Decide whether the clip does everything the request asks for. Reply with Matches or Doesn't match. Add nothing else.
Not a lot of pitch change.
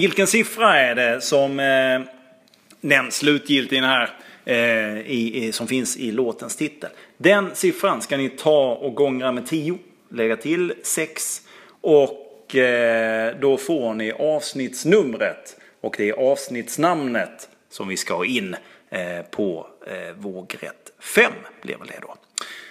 Doesn't match